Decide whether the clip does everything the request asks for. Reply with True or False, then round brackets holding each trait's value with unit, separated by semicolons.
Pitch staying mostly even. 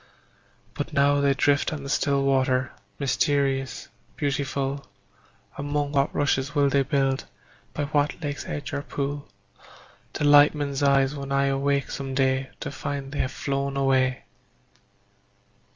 True (1.0 semitones)